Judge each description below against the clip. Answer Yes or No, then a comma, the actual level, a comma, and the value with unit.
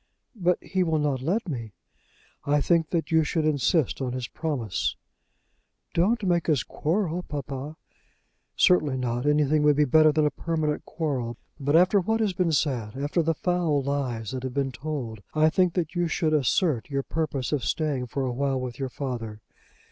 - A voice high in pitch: No, medium, 150 Hz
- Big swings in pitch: No, average, 3.8 semitones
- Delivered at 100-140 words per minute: No, average, 180 wpm